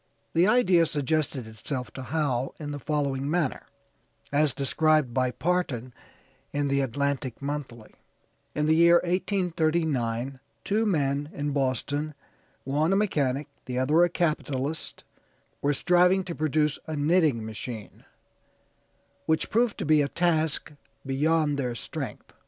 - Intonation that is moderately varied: Yes, average, 3.3 semitones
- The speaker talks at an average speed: No, slow, 130 wpm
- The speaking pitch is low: No, medium, 145 Hz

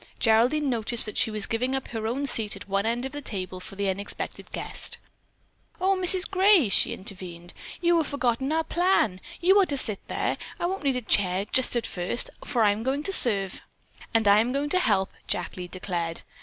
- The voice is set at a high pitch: Yes, high, 230 Hz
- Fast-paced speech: Yes, fast, 210 wpm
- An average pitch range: No, wide, 6.4 semitones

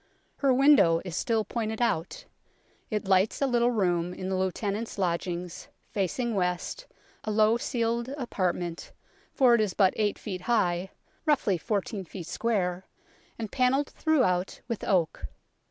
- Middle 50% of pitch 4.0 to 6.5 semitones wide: Yes, average, 4.6 semitones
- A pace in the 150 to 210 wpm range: No, average, 140 wpm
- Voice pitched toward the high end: Yes, high, 210 Hz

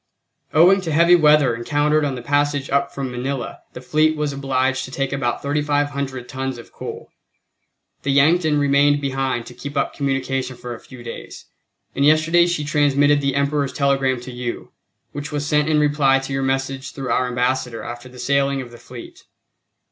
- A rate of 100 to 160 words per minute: No, average, 180 wpm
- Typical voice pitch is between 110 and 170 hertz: Yes, medium, 140 Hz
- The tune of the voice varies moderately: No, narrow, 2.0 semitones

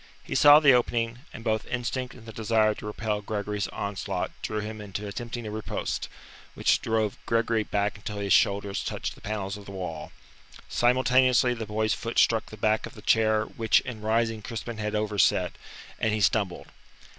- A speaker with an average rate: Yes, average, 180 wpm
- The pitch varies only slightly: Yes, narrow, 1.8 semitones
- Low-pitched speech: Yes, low, 110 Hz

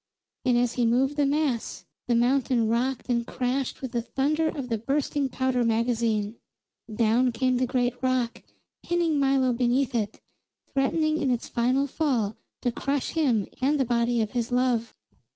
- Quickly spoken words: No, average, 165 wpm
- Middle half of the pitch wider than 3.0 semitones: No, narrow, 2.6 semitones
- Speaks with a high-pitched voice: Yes, very high, 250 Hz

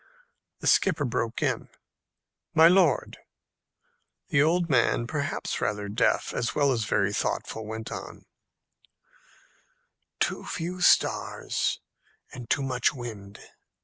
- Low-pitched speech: Yes, low, 125 Hz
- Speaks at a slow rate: Yes, slow, 115 wpm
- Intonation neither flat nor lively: No, wide, 5.7 semitones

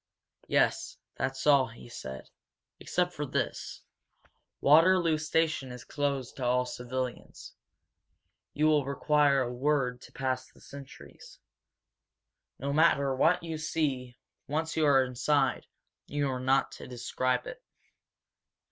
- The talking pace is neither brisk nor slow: No, slow, 125 wpm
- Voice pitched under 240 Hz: Yes, medium, 140 Hz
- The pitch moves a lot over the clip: No, average, 3.2 semitones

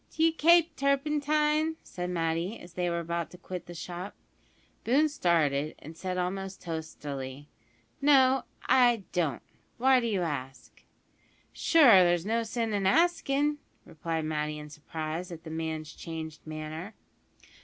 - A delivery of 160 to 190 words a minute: No, average, 140 wpm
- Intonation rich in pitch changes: Yes, wide, 8.4 semitones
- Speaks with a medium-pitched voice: Yes, medium, 180 Hz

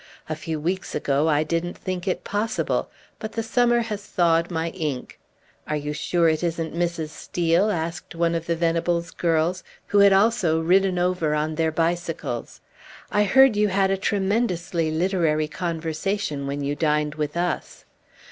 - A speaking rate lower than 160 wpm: No, average, 165 wpm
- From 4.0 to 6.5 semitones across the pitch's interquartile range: No, average, 3.3 semitones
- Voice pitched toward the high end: No, medium, 170 Hz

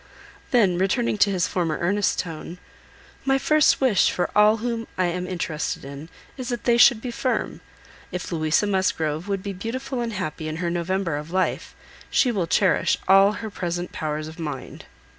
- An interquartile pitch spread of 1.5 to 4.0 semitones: No, average, 5.0 semitones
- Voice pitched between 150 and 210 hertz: Yes, medium, 185 Hz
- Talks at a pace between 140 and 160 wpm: No, average, 175 wpm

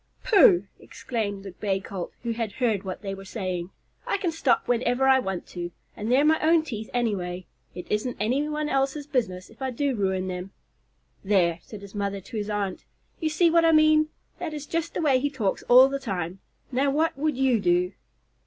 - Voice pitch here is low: No, high, 230 Hz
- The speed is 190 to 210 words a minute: Yes, average, 200 wpm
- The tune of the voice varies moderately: No, wide, 6.7 semitones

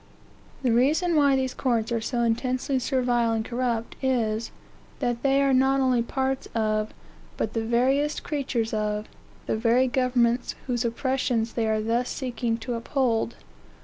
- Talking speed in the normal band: Yes, average, 150 wpm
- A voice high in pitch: Yes, high, 245 Hz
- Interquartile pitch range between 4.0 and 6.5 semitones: No, narrow, 2.5 semitones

